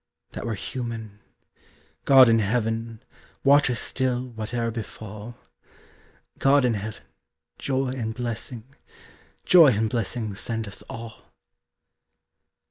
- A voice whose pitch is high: No, low, 115 Hz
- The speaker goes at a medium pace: No, slow, 110 wpm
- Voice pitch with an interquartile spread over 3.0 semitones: No, narrow, 2.4 semitones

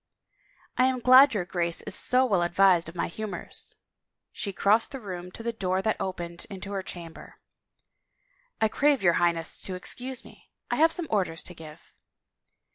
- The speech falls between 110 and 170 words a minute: No, average, 190 wpm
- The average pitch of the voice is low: No, high, 195 Hz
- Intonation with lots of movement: Yes, wide, 6.2 semitones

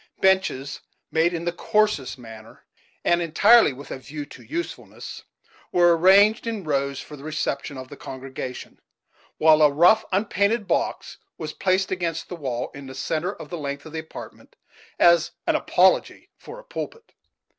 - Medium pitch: Yes, medium, 160 Hz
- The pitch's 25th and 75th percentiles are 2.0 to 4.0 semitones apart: No, average, 5.3 semitones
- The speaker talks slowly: No, average, 165 wpm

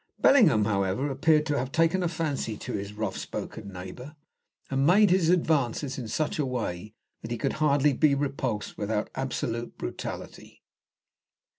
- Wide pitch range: Yes, wide, 5.9 semitones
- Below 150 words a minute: No, average, 155 wpm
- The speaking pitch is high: No, low, 135 Hz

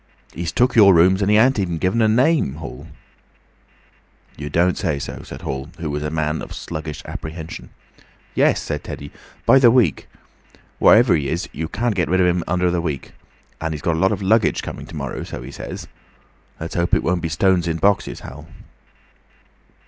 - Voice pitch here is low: Yes, very low, 85 Hz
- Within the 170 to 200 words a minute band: Yes, average, 195 wpm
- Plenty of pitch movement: No, average, 4.1 semitones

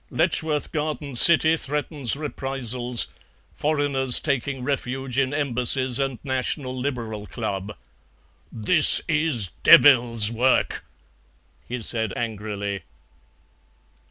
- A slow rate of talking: Yes, slow, 90 wpm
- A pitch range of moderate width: Yes, average, 3.7 semitones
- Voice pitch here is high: No, low, 130 Hz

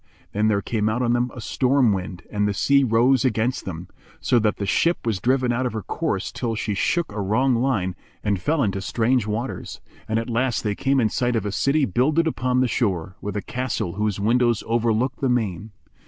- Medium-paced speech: No, fast, 215 wpm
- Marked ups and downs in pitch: No, average, 3.6 semitones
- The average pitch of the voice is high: No, low, 115 Hz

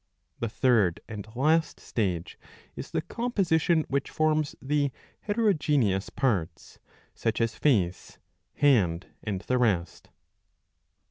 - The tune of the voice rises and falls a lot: Yes, wide, 7.9 semitones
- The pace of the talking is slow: Yes, slow, 110 wpm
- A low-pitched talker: Yes, low, 125 Hz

